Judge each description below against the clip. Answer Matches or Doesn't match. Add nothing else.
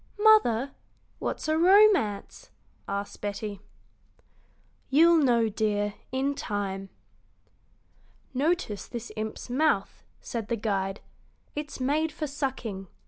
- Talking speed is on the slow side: Matches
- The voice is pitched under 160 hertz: Doesn't match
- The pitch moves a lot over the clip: Matches